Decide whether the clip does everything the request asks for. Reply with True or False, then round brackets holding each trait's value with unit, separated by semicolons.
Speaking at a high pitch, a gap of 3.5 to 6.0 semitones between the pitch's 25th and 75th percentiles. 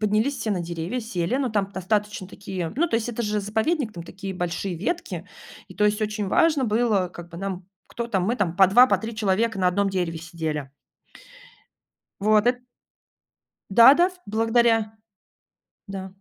True (210 Hz; 3.8 semitones)